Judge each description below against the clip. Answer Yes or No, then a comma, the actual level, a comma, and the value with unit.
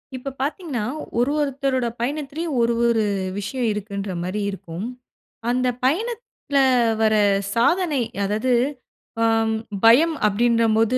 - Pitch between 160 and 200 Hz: No, very high, 250 Hz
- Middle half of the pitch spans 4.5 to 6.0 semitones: Yes, average, 4.8 semitones